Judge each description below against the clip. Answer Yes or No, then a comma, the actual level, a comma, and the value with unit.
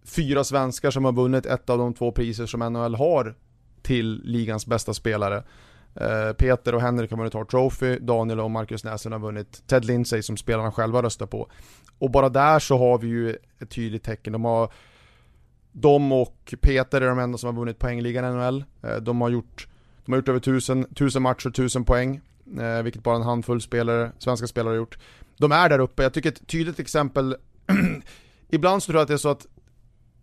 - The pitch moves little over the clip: Yes, narrow, 2.2 semitones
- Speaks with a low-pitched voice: Yes, low, 120 Hz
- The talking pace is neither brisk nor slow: No, fast, 200 wpm